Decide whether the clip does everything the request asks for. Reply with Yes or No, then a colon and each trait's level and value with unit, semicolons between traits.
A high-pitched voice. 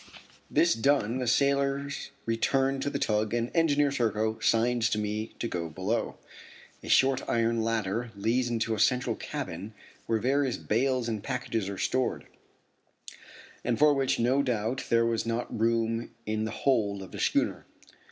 No: low, 115 Hz